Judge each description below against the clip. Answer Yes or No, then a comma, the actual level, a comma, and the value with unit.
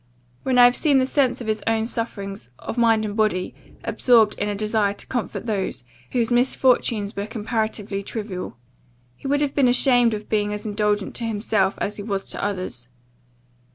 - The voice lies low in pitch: No, high, 215 Hz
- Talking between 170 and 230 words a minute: Yes, average, 185 wpm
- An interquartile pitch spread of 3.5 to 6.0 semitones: No, average, 2.9 semitones